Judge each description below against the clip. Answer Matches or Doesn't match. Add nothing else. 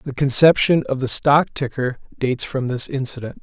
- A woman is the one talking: Doesn't match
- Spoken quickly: Doesn't match